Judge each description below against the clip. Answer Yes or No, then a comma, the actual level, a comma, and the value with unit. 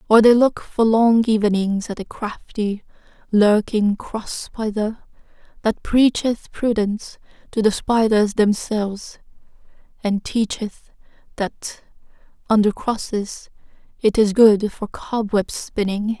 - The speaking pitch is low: No, high, 215 Hz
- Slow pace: Yes, slow, 110 wpm